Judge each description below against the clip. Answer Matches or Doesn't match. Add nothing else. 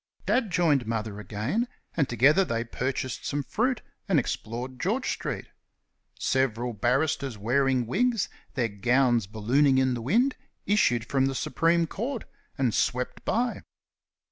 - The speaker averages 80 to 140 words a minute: Matches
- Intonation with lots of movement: Matches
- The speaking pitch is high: Doesn't match